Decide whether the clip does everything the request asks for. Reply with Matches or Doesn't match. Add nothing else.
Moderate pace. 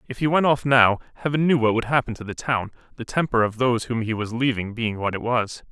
Doesn't match